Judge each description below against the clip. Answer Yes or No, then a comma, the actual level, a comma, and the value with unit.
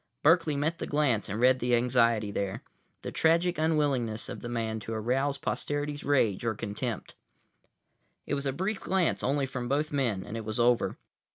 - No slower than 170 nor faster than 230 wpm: Yes, average, 180 wpm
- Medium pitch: No, low, 130 Hz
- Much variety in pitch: No, average, 4.4 semitones